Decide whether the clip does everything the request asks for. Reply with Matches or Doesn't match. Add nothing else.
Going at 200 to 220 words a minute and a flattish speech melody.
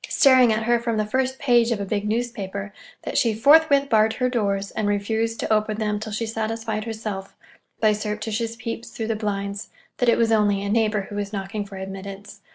Matches